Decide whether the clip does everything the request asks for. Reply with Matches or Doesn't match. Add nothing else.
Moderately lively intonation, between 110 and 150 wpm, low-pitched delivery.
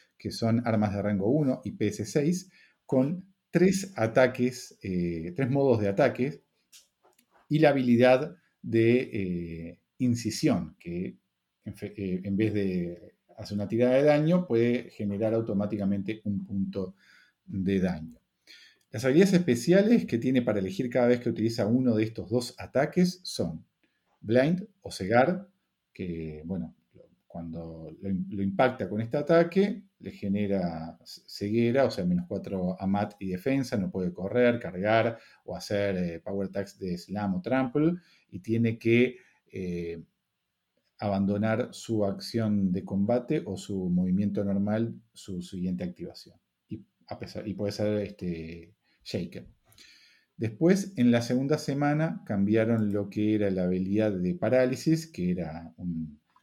Matches